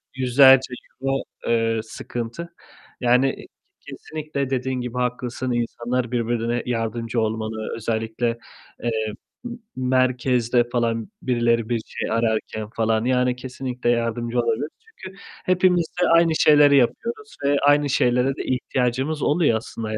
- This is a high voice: No, low, 125 Hz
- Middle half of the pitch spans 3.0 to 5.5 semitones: No, narrow, 2.6 semitones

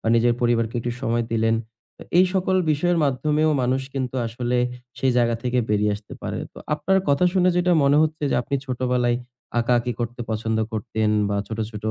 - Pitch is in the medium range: No, low, 125 Hz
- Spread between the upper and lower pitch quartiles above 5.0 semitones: No, average, 3.8 semitones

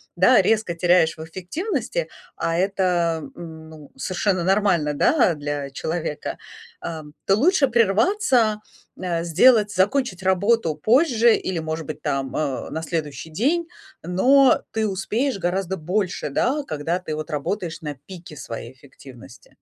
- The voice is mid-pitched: Yes, medium, 180 Hz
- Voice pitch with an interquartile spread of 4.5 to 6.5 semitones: Yes, average, 5.3 semitones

